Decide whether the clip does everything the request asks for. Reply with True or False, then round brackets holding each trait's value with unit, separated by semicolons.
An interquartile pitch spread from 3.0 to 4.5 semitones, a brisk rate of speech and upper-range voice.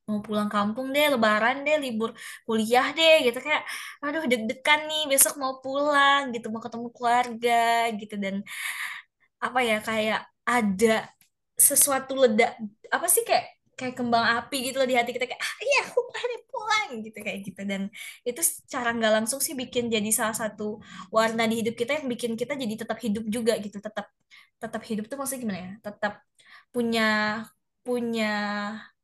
True (3.7 semitones; 170 wpm; 235 Hz)